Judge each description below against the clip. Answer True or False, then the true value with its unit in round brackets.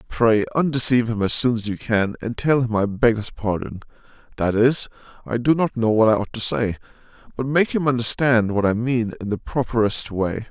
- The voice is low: True (115 Hz)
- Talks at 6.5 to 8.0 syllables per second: False (5.3 syllables/s)